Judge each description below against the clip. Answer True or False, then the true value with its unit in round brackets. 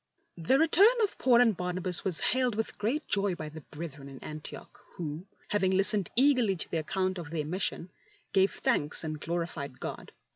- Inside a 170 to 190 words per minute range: True (180 wpm)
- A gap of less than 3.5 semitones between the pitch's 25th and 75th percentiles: False (5.5 semitones)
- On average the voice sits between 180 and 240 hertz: True (185 Hz)